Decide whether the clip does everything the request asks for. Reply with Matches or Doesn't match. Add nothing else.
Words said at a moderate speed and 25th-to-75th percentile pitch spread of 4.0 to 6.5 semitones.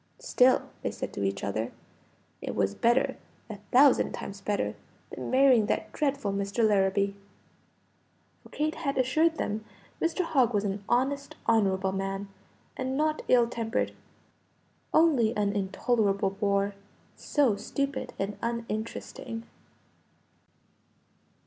Doesn't match